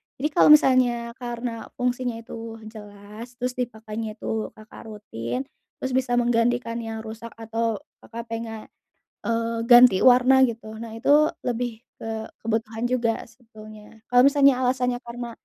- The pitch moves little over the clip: Yes, narrow, 1.9 semitones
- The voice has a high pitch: Yes, high, 230 Hz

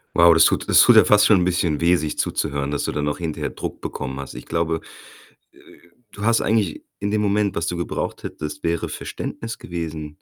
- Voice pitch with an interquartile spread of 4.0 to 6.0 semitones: Yes, average, 4.7 semitones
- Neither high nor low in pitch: No, very low, 85 Hz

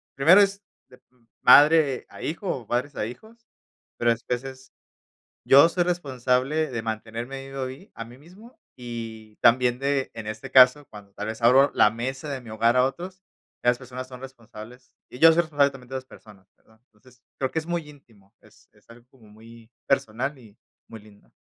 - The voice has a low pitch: Yes, low, 125 Hz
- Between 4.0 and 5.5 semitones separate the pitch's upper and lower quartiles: No, average, 3.6 semitones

